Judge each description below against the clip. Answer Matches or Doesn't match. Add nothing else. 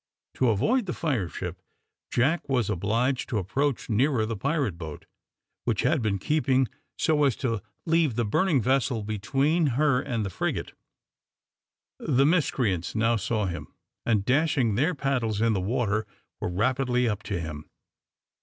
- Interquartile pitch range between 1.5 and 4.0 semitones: Doesn't match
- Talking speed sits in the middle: Matches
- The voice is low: Matches